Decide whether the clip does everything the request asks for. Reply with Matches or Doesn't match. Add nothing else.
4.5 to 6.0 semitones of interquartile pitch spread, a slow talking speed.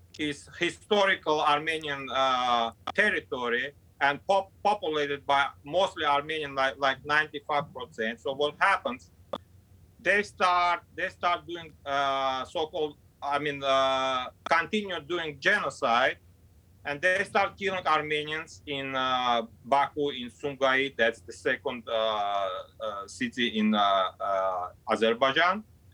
Matches